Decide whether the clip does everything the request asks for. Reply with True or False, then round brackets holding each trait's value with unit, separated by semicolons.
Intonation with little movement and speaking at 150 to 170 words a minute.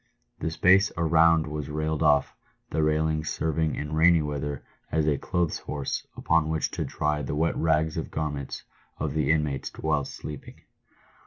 True (1.3 semitones; 160 wpm)